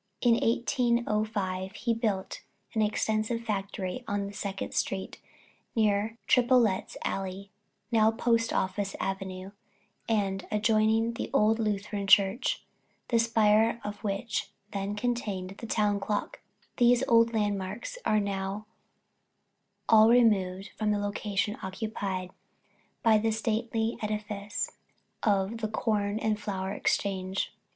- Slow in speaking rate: Yes, slow, 115 wpm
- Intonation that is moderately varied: No, narrow, 2.3 semitones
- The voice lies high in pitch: Yes, high, 210 Hz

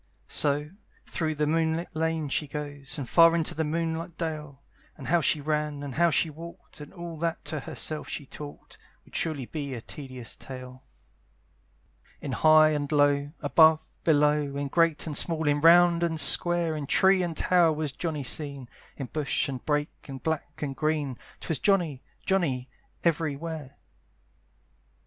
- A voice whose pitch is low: No, medium, 150 Hz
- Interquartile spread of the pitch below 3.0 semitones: Yes, narrow, 2.4 semitones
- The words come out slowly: No, average, 165 wpm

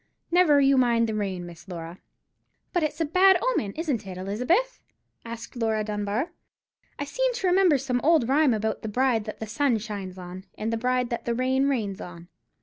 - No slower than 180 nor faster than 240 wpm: Yes, average, 195 wpm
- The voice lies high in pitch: Yes, high, 235 Hz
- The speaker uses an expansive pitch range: Yes, wide, 5.7 semitones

